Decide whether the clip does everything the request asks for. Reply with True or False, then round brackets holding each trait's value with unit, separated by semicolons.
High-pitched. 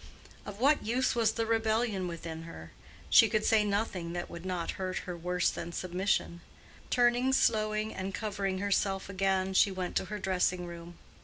True (195 Hz)